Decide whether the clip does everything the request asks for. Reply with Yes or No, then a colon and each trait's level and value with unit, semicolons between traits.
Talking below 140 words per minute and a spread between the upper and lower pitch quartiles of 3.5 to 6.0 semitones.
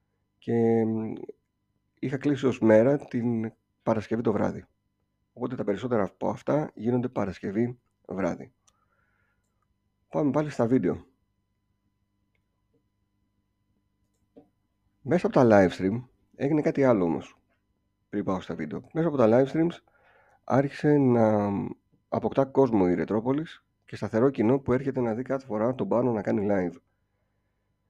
Yes: average, 125 wpm; average, 4.2 semitones